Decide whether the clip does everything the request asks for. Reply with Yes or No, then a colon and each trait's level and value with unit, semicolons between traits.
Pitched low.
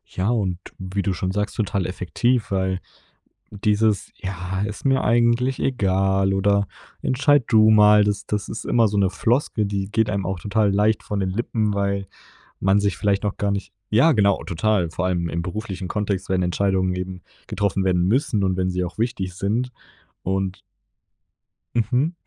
Yes: low, 100 Hz